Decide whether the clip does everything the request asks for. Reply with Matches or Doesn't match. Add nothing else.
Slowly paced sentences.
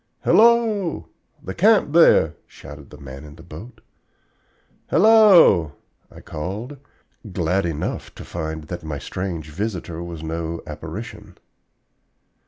Matches